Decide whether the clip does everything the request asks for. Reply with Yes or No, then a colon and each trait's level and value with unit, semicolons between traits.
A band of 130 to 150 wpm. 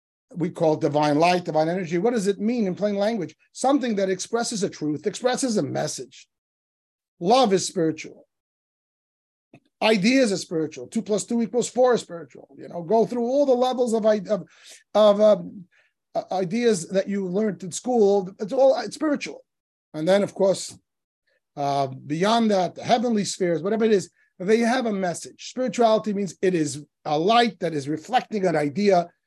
No: average, 170 wpm